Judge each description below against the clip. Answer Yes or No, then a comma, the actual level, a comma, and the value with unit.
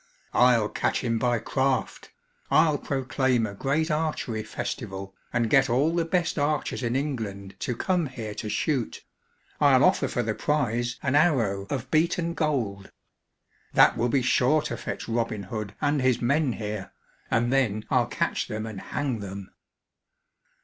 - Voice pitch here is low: Yes, low, 125 Hz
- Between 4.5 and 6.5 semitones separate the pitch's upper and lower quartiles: Yes, average, 4.9 semitones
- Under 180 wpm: Yes, average, 155 wpm